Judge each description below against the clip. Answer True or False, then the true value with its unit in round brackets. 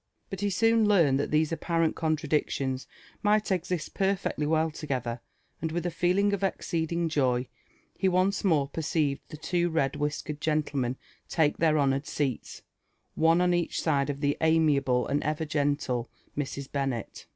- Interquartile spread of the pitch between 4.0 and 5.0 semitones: False (3.5 semitones)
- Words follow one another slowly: False (150 wpm)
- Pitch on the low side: False (155 Hz)